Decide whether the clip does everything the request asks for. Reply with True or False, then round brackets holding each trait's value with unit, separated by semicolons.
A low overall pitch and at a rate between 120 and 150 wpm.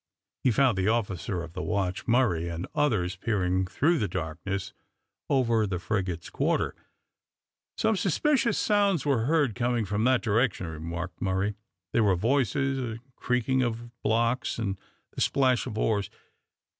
True (110 Hz; 145 wpm)